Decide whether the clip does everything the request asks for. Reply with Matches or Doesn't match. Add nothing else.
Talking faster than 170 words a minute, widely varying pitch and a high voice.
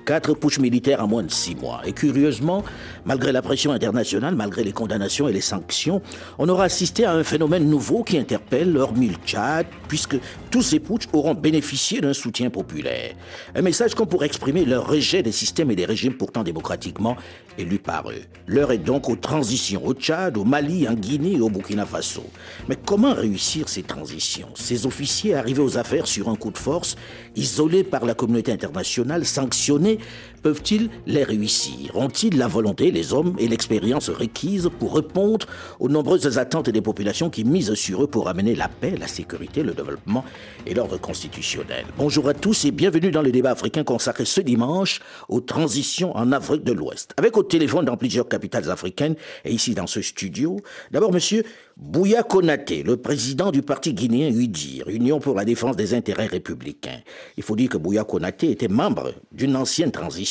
Doesn't match